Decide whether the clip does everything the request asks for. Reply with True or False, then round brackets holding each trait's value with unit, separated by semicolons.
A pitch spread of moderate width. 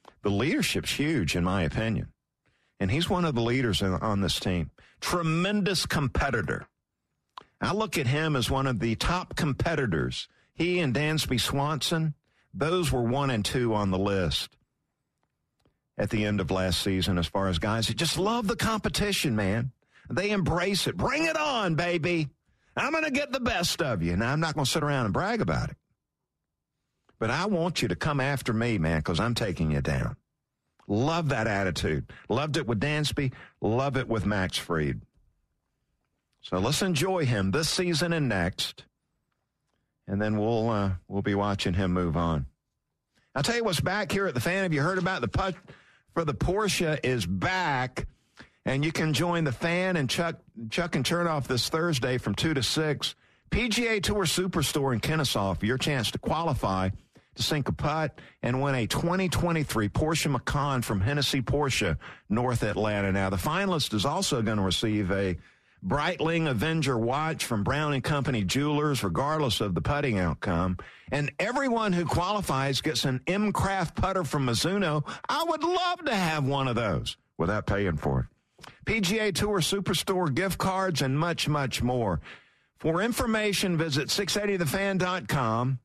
False (8.0 semitones)